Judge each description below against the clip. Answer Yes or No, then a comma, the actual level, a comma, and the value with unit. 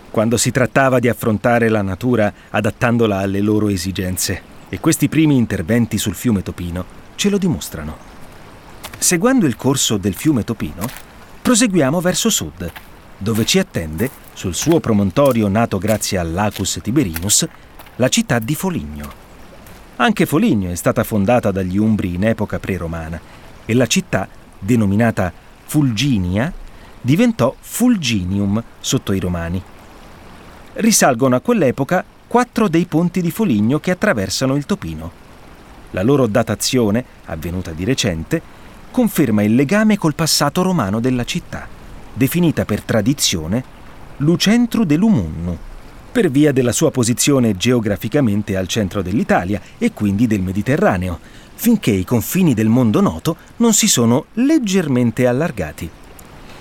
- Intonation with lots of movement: Yes, wide, 7.1 semitones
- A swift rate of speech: No, average, 125 wpm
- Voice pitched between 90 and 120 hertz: Yes, low, 115 Hz